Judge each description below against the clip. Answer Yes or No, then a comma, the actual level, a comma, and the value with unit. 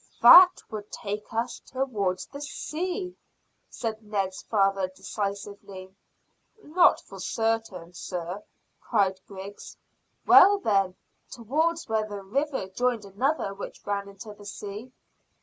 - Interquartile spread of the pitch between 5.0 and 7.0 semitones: No, average, 4.3 semitones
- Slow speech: Yes, slow, 115 wpm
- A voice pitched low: No, high, 210 Hz